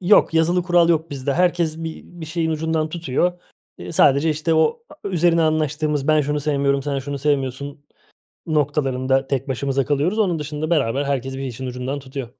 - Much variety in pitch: No, average, 3.0 semitones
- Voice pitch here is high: No, medium, 150 Hz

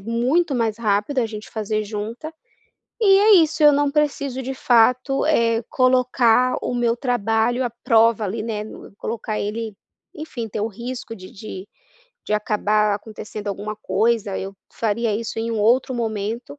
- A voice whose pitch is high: Yes, high, 230 Hz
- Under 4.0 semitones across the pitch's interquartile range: Yes, average, 3.0 semitones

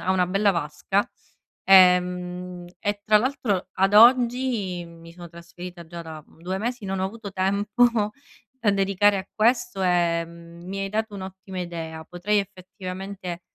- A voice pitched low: No, high, 190 Hz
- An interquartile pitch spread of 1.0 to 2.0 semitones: No, narrow, 2.6 semitones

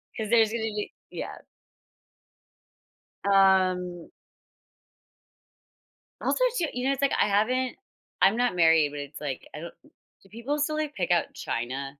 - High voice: Yes, high, 200 Hz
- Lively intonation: Yes, wide, 6.7 semitones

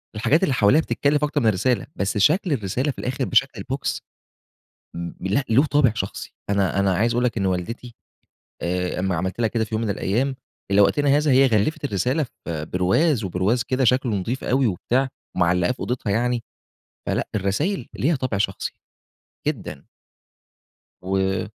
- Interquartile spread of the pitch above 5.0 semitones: Yes, wide, 5.6 semitones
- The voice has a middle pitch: No, low, 115 Hz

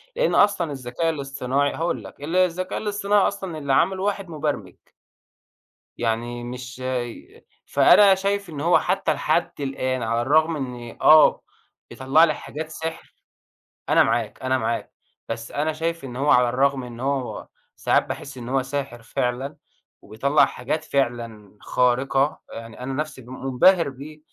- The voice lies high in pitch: No, medium, 140 Hz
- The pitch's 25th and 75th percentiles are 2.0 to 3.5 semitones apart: No, average, 4.4 semitones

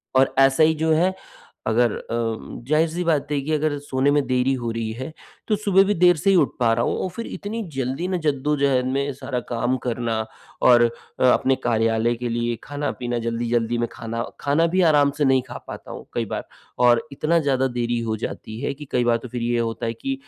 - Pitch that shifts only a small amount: No, average, 4.4 semitones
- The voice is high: No, low, 130 Hz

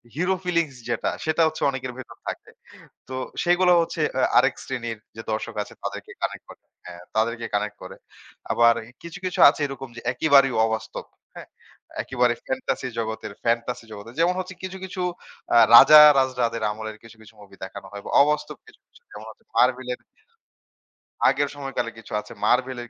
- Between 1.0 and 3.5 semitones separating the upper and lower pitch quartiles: No, average, 4.8 semitones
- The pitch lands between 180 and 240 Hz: No, low, 125 Hz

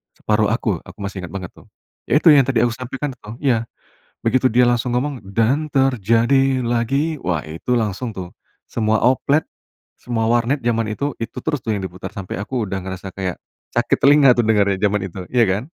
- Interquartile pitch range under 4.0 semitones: No, average, 4.5 semitones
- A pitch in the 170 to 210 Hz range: No, low, 115 Hz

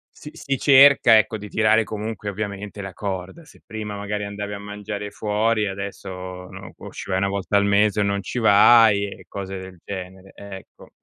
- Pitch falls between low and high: No, low, 100 Hz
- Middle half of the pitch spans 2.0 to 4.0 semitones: No, narrow, 1.5 semitones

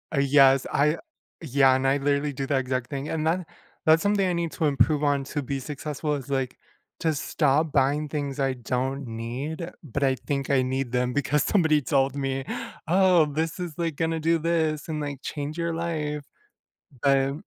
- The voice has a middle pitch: Yes, medium, 145 Hz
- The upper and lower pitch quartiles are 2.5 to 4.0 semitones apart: Yes, average, 2.8 semitones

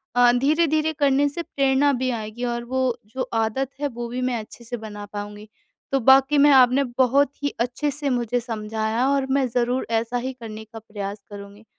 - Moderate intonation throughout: Yes, average, 3.5 semitones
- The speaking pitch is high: Yes, high, 245 Hz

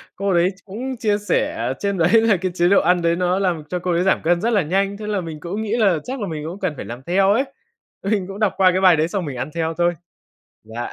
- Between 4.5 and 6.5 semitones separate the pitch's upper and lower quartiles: No, average, 3.0 semitones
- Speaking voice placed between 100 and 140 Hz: No, medium, 185 Hz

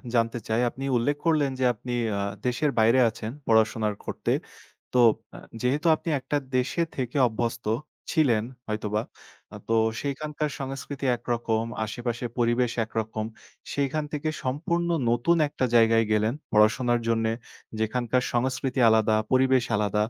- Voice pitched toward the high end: No, low, 120 Hz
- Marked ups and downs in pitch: No, average, 3.3 semitones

